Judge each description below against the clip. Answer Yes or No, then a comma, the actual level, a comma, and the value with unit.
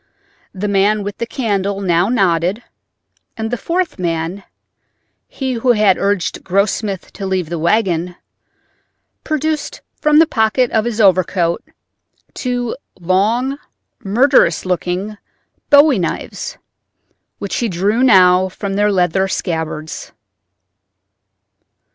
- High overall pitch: Yes, high, 200 Hz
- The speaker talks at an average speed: No, slow, 105 wpm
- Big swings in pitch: No, average, 4.5 semitones